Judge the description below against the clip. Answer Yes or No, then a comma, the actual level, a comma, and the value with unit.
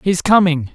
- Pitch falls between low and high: Yes, medium, 170 Hz